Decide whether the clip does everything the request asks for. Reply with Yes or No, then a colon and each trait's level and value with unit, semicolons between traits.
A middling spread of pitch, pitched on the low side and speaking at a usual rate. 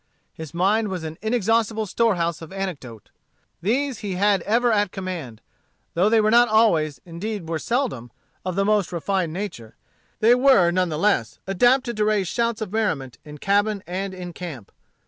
No: average, 4.5 semitones; high, 195 Hz; average, 170 wpm